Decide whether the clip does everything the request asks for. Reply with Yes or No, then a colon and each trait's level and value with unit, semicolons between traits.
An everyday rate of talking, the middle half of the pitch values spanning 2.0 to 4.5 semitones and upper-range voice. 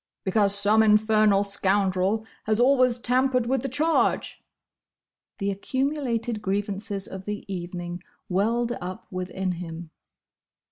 No: slow, 110 wpm; average, 3.7 semitones; high, 205 Hz